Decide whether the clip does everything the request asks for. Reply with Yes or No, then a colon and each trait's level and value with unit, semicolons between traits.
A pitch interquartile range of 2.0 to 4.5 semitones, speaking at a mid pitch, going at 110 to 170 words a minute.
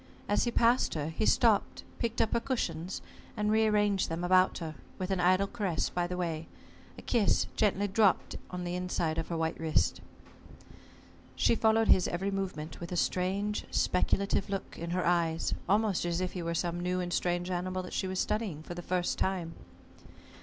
No: average, 2.8 semitones; medium, 180 Hz; average, 190 wpm